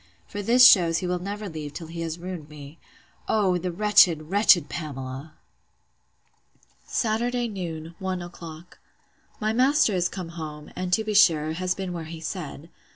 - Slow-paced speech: No, average, 155 wpm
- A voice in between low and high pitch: Yes, medium, 175 Hz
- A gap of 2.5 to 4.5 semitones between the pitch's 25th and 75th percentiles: Yes, average, 4.1 semitones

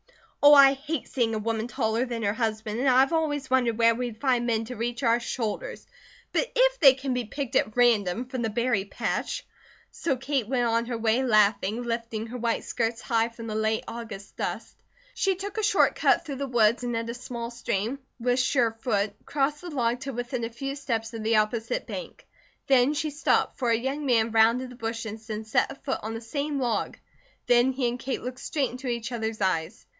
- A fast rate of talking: Yes, fast, 215 wpm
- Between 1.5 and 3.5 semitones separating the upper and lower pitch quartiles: Yes, average, 2.8 semitones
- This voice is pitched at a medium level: No, high, 240 Hz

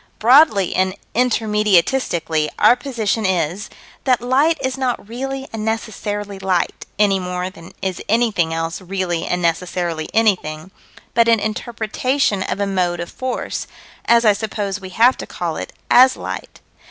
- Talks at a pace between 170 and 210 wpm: No, average, 150 wpm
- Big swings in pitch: No, average, 4.4 semitones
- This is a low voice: No, high, 205 Hz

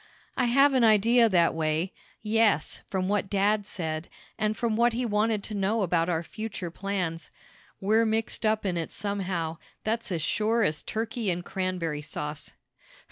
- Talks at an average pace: Yes, average, 165 wpm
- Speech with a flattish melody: No, average, 4.5 semitones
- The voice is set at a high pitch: Yes, high, 200 Hz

